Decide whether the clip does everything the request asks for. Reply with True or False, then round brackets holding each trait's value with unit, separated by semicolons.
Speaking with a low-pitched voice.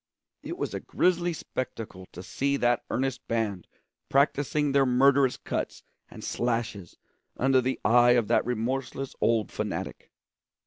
True (125 Hz)